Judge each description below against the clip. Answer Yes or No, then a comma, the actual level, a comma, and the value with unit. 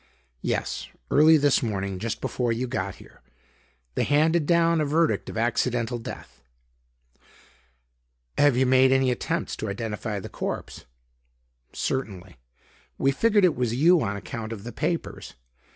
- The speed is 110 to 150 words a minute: Yes, average, 140 wpm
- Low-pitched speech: Yes, low, 125 Hz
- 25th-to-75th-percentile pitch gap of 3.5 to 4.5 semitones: No, average, 5.1 semitones